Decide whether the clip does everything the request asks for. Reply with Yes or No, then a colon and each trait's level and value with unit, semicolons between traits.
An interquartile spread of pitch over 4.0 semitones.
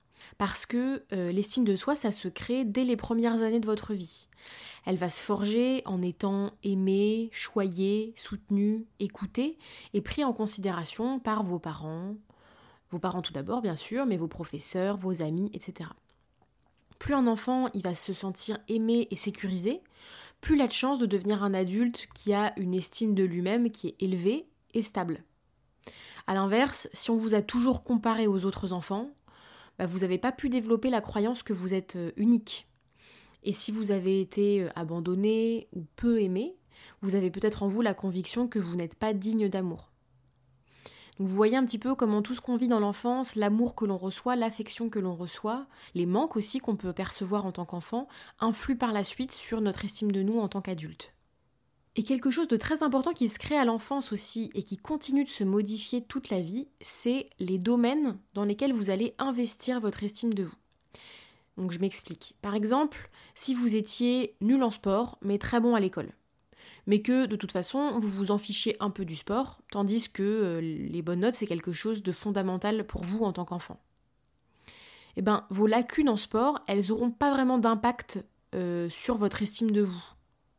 No: average, 3.7 semitones